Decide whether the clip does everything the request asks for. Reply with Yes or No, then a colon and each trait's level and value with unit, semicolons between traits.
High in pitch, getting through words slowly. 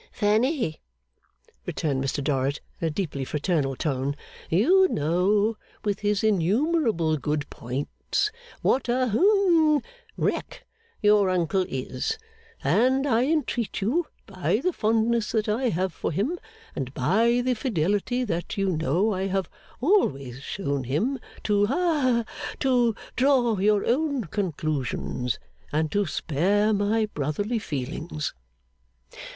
Yes: high, 205 Hz; slow, 125 wpm